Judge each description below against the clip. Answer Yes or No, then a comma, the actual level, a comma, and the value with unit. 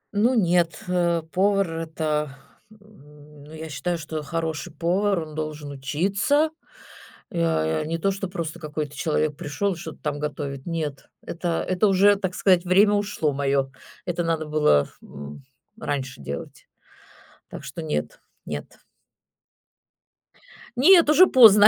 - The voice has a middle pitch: Yes, medium, 165 Hz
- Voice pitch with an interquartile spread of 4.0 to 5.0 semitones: Yes, average, 4.7 semitones